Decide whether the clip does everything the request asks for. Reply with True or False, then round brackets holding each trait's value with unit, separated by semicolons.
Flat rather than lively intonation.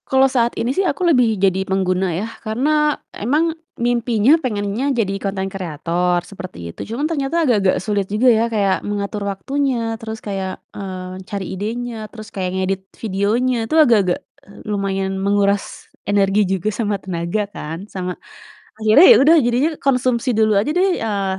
False (4.0 semitones)